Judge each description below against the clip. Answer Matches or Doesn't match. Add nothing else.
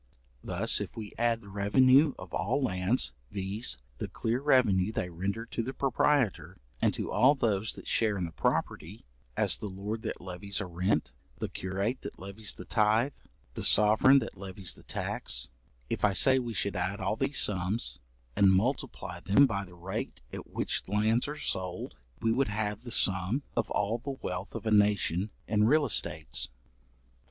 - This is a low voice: Matches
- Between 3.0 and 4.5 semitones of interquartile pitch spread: Matches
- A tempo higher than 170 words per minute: Matches